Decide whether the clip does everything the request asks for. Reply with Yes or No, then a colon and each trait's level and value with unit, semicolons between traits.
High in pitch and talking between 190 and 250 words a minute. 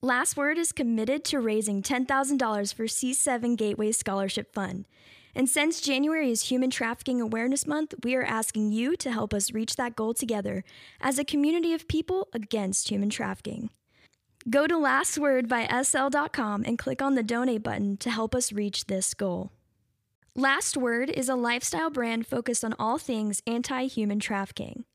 No: high, 240 Hz; average, 165 wpm